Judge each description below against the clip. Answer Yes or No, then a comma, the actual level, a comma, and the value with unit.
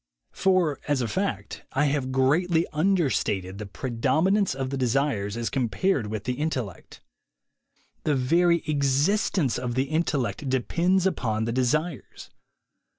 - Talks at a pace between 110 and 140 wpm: Yes, slow, 135 wpm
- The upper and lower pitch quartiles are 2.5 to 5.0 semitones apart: No, wide, 5.5 semitones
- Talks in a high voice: No, low, 135 Hz